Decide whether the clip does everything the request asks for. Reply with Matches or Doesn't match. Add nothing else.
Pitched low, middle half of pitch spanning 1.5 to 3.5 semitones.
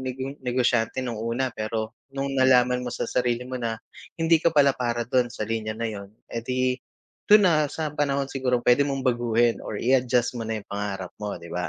Matches